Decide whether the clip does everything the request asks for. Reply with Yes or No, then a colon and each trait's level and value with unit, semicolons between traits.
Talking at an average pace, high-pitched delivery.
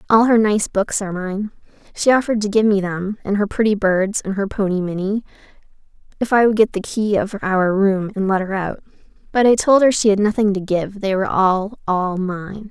No: fast, 220 wpm; high, 200 Hz